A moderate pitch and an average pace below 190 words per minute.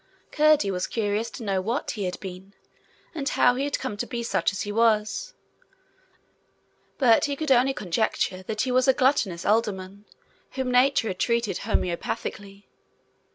No: high, 225 Hz; average, 160 wpm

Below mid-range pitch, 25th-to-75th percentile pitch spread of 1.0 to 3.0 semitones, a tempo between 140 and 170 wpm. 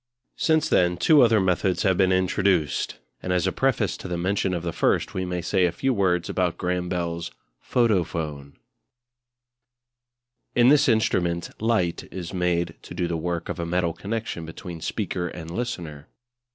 Yes: very low, 90 Hz; narrow, 2.5 semitones; average, 165 wpm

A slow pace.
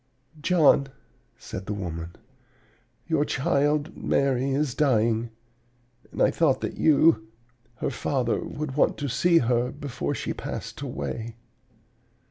Yes: slow, 120 wpm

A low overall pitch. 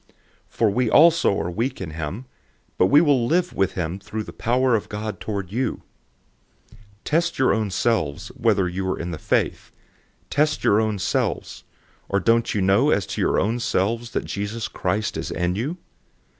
Yes: low, 110 Hz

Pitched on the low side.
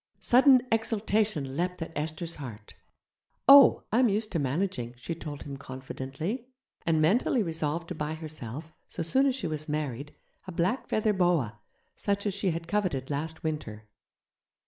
No: medium, 165 Hz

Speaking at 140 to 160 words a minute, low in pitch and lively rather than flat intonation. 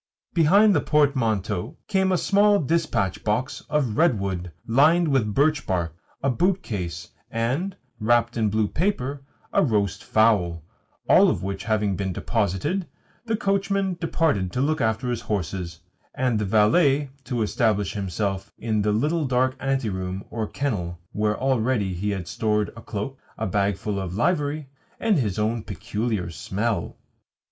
Yes: average, 150 wpm; low, 115 Hz; wide, 6.3 semitones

